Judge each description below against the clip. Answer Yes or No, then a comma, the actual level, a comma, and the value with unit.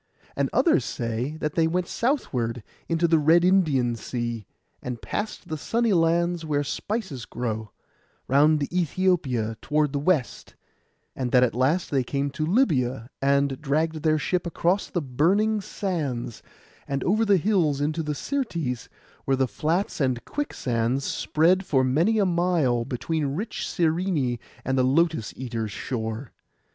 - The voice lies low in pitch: No, medium, 150 Hz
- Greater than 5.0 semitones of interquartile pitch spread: Yes, wide, 5.5 semitones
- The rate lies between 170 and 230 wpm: No, average, 150 wpm